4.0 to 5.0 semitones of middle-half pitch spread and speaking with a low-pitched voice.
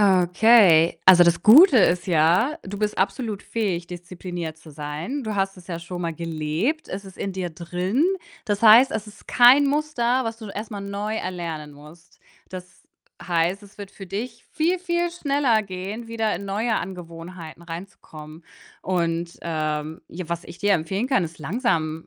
No: average, 4.7 semitones; medium, 185 Hz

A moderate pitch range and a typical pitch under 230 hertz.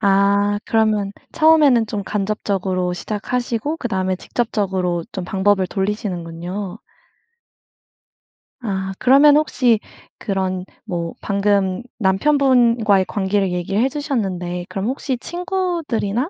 Yes: average, 4.3 semitones; high, 205 Hz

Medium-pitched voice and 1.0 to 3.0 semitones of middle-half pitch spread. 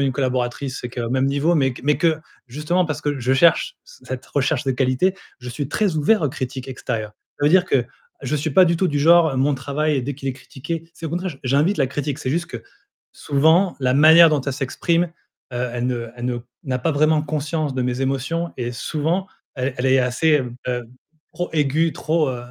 No: medium, 145 Hz; average, 3.7 semitones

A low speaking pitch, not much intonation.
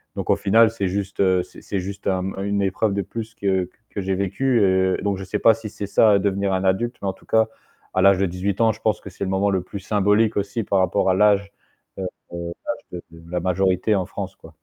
Yes: low, 100 Hz; narrow, 1.7 semitones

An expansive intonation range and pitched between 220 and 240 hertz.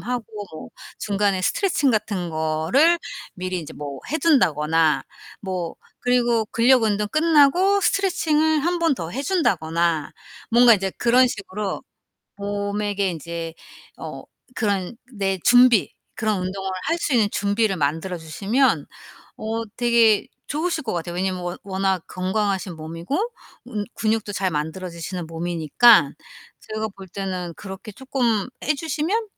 No: wide, 5.7 semitones; high, 205 Hz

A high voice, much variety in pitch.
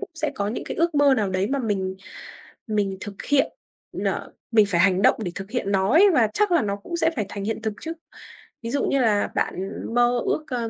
Yes: high, 225 Hz; wide, 6.0 semitones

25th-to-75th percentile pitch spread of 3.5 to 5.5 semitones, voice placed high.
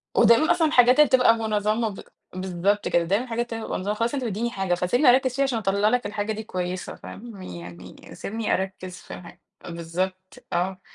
Yes: average, 4.3 semitones; high, 210 Hz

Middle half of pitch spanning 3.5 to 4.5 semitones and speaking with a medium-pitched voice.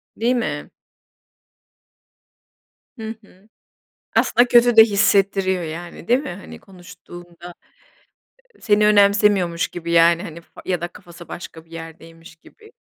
Yes: average, 3.8 semitones; medium, 180 Hz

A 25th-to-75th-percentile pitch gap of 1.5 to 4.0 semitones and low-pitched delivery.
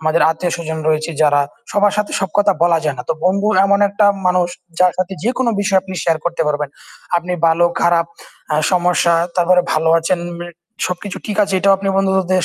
No: average, 2.7 semitones; medium, 180 Hz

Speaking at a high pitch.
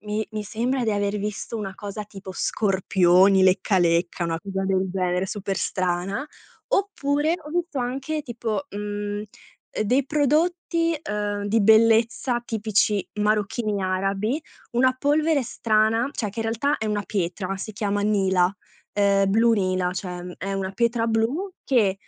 Yes: high, 210 Hz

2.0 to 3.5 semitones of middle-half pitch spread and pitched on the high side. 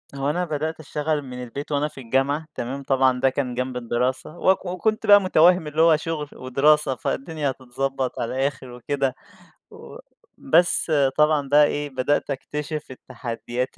No: average, 2.9 semitones; medium, 140 Hz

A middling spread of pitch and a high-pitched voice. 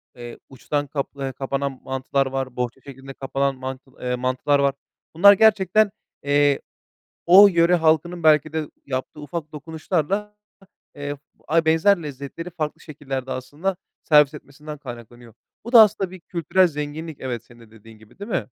No: average, 4.0 semitones; medium, 145 Hz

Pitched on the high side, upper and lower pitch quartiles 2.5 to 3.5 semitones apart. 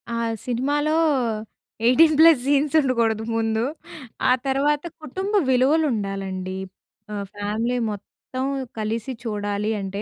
No: high, 235 Hz; wide, 5.6 semitones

